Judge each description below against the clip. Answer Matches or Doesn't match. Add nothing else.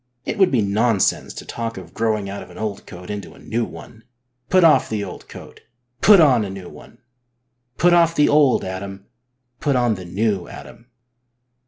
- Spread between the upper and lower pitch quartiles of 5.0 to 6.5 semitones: Matches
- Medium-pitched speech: Doesn't match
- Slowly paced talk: Doesn't match